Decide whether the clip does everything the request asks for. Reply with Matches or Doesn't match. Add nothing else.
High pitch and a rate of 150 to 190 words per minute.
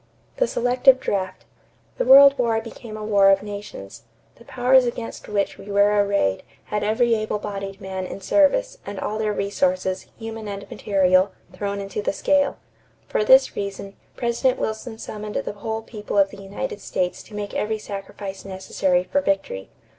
Matches